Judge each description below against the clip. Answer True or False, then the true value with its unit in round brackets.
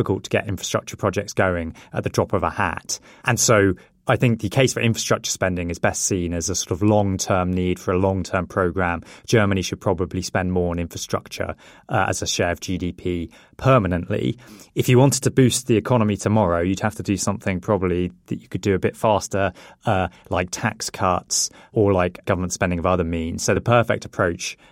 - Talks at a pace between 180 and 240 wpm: True (205 wpm)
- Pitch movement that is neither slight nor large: True (3.4 semitones)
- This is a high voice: False (100 Hz)